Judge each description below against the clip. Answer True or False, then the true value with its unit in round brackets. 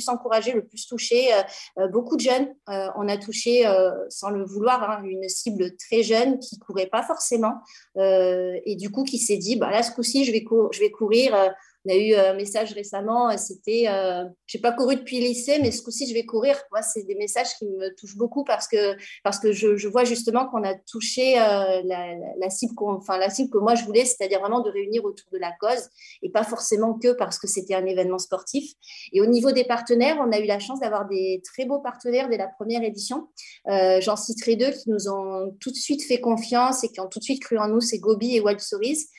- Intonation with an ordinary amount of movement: True (3.5 semitones)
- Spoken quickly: True (245 wpm)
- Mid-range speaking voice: False (220 Hz)